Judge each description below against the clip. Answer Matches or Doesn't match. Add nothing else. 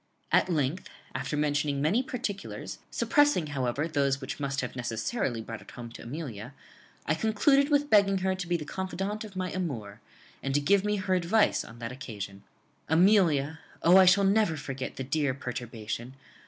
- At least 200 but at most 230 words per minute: Doesn't match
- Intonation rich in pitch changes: Matches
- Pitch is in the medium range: Matches